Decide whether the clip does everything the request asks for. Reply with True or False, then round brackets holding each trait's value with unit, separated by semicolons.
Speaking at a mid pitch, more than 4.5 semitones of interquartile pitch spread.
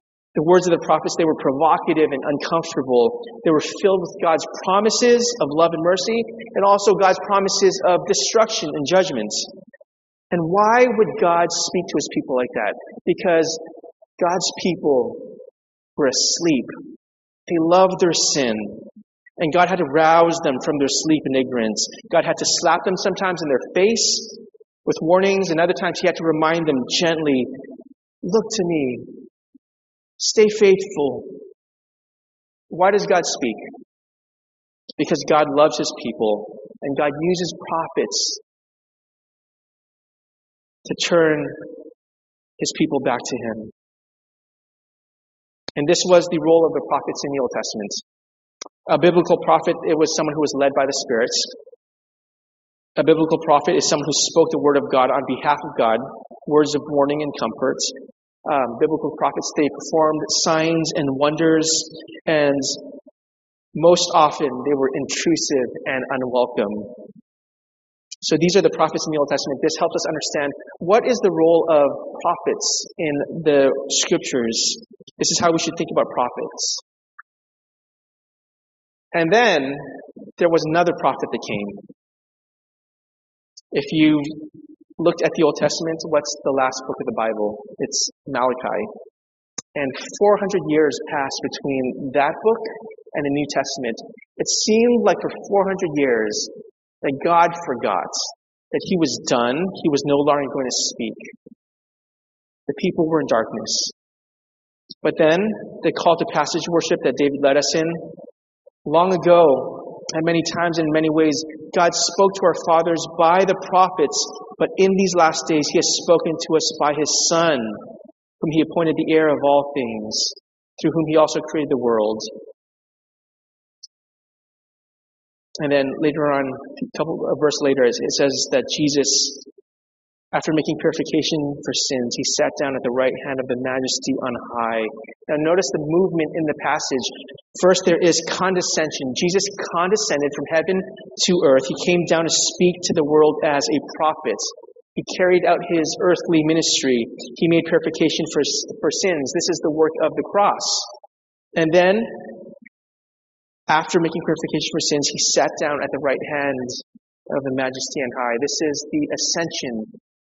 False (160 Hz; 4.1 semitones)